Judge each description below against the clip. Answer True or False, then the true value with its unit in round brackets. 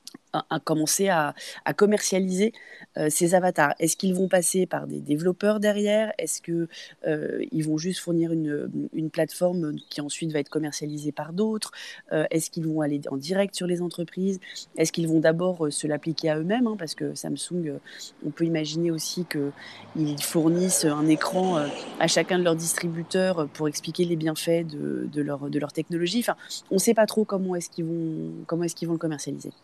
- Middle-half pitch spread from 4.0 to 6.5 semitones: False (3.2 semitones)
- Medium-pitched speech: True (165 Hz)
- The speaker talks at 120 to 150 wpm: False (190 wpm)